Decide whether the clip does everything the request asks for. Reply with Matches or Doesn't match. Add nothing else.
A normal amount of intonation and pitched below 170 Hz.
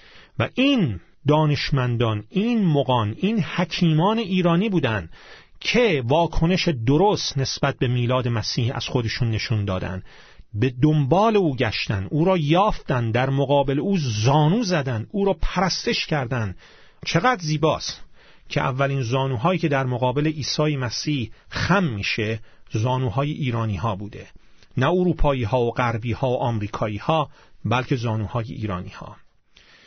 Doesn't match